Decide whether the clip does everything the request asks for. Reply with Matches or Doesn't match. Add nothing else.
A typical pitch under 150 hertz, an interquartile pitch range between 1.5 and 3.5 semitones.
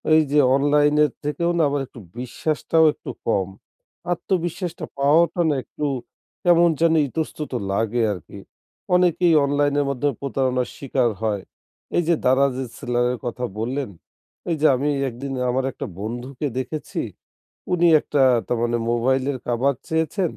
Doesn't match